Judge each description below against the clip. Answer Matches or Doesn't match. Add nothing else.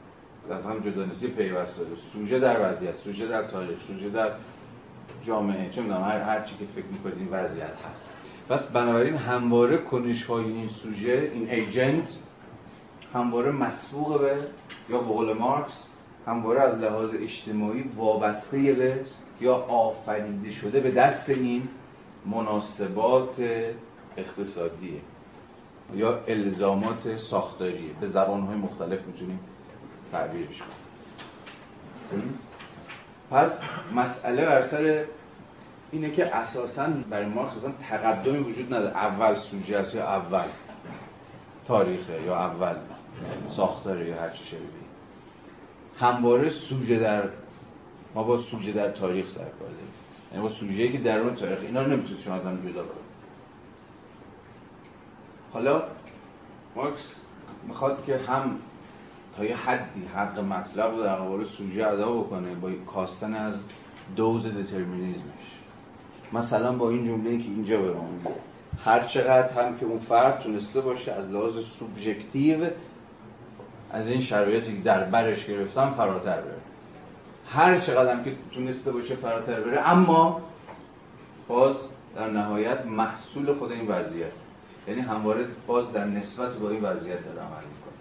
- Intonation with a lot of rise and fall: Doesn't match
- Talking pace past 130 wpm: Doesn't match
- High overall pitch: Doesn't match